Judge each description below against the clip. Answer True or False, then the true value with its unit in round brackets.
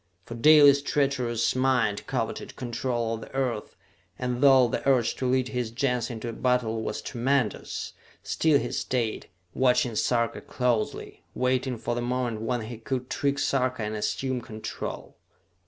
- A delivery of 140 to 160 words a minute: True (150 wpm)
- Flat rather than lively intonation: True (2.0 semitones)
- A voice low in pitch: True (125 Hz)